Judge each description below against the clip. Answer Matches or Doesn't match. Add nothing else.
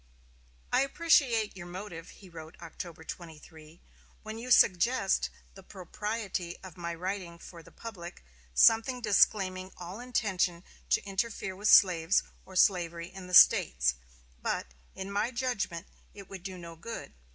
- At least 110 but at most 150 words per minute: Matches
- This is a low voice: Doesn't match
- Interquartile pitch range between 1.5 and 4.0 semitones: Matches